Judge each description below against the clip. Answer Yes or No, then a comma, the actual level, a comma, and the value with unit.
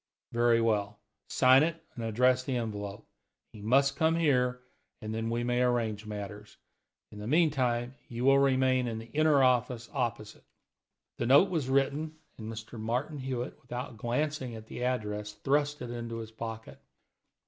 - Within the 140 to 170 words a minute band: Yes, average, 160 wpm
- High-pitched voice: No, low, 120 Hz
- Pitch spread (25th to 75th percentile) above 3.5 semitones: No, average, 3.2 semitones